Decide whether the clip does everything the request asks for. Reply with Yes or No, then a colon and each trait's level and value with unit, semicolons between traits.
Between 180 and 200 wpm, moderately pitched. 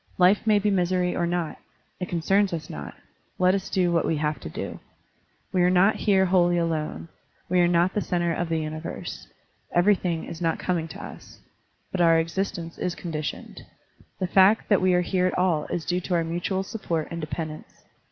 Yes: average, 195 wpm; medium, 175 Hz